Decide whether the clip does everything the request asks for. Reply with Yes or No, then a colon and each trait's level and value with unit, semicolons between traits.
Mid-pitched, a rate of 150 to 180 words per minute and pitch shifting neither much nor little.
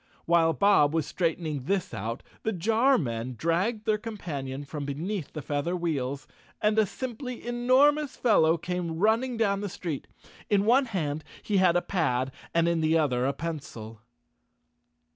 No: medium, 170 Hz; average, 160 wpm; wide, 6.7 semitones